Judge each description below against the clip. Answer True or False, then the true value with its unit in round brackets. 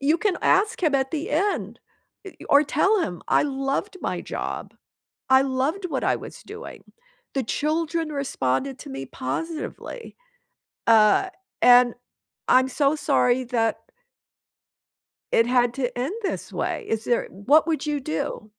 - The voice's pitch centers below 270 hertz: False (275 Hz)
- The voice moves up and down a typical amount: True (4.9 semitones)